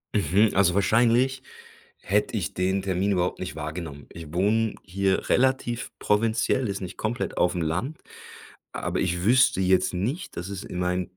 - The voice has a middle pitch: No, very low, 95 Hz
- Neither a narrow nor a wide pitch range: Yes, average, 3.9 semitones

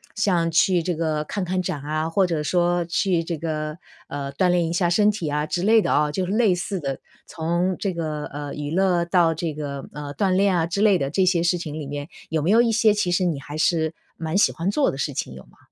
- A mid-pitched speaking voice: Yes, medium, 170 Hz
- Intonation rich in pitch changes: No, average, 3.4 semitones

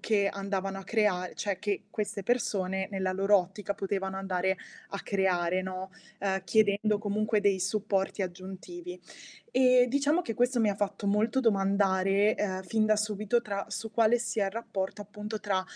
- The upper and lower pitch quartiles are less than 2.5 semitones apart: Yes, narrow, 2.0 semitones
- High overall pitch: Yes, high, 200 Hz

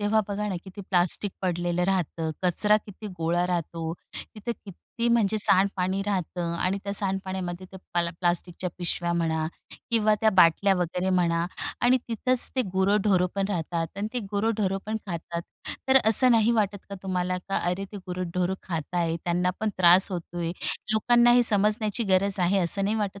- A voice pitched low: No, high, 190 Hz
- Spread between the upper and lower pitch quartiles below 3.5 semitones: Yes, average, 3.0 semitones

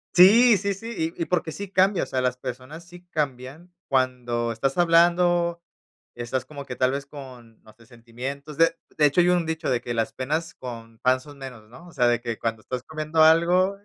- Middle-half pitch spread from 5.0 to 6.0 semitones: Yes, wide, 5.4 semitones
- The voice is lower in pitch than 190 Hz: Yes, medium, 140 Hz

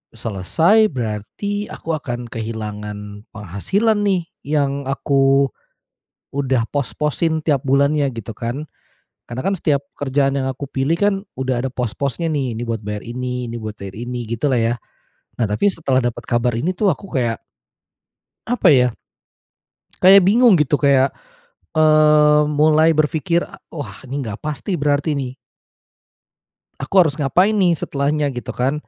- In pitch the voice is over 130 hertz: Yes, medium, 140 Hz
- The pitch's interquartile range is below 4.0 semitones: No, average, 4.4 semitones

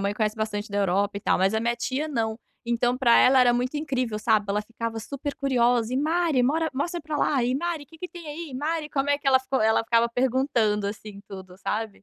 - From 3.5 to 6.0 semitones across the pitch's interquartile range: Yes, average, 4.8 semitones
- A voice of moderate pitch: No, high, 245 Hz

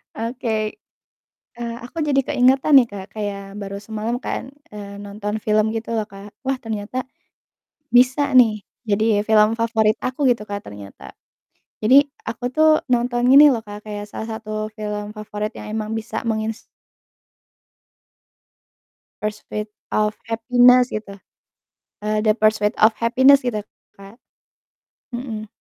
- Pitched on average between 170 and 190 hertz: No, high, 220 Hz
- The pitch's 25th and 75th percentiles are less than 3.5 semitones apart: Yes, narrow, 2.6 semitones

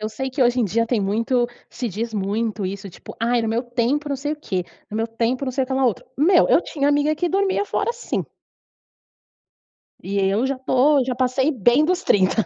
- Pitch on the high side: Yes, very high, 250 Hz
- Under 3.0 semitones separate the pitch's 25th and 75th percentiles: No, average, 4.1 semitones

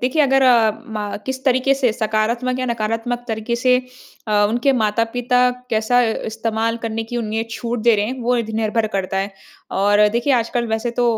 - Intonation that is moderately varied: No, narrow, 2.2 semitones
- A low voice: No, high, 230 Hz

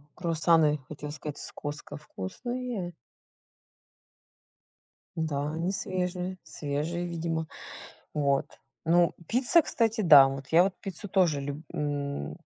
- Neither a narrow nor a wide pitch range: Yes, average, 3.9 semitones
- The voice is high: No, medium, 160 Hz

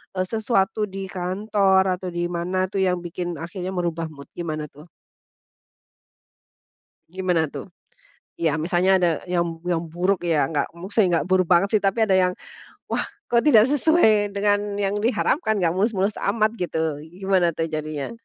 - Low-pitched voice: No, medium, 185 Hz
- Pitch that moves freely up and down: No, average, 2.9 semitones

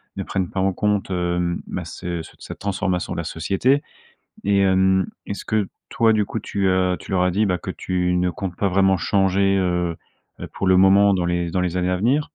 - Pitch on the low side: Yes, very low, 95 Hz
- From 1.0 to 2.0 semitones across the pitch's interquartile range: Yes, narrow, 1.7 semitones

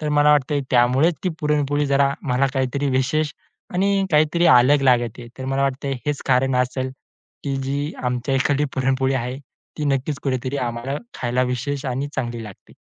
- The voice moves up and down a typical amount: No, narrow, 2.3 semitones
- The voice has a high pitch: No, low, 135 Hz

